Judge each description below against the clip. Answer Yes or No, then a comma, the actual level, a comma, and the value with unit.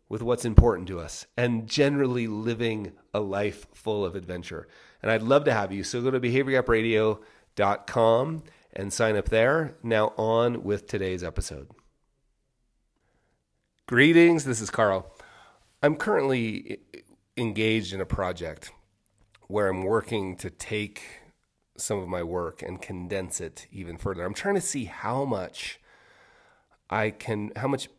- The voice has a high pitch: No, low, 110 Hz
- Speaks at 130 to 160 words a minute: Yes, average, 140 wpm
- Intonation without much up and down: No, average, 3.7 semitones